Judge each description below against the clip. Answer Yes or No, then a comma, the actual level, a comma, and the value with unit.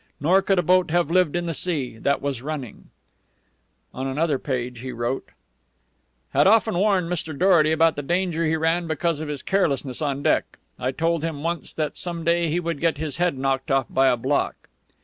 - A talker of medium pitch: Yes, medium, 160 Hz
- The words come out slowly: No, average, 200 wpm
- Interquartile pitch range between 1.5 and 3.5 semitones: No, average, 4.0 semitones